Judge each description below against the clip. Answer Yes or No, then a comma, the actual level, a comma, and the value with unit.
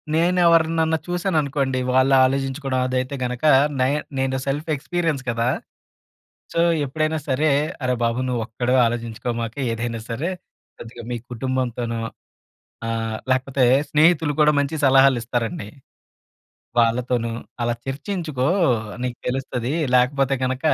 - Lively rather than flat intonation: No, average, 3.6 semitones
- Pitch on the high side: No, low, 130 Hz